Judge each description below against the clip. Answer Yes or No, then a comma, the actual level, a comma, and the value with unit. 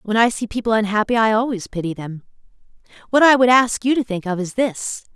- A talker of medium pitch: No, high, 220 Hz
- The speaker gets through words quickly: Yes, fast, 220 wpm